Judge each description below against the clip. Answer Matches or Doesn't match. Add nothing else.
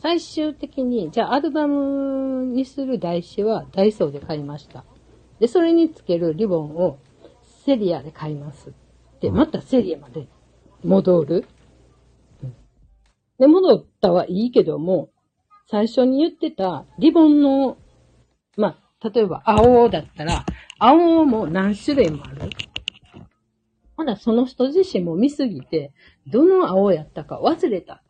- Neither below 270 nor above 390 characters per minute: Doesn't match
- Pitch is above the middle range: Matches